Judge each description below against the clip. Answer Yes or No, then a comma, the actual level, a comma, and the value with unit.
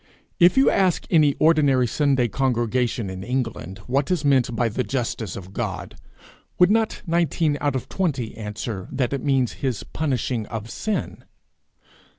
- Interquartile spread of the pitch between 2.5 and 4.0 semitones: No, average, 4.7 semitones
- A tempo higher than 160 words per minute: No, average, 155 wpm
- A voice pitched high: No, low, 130 Hz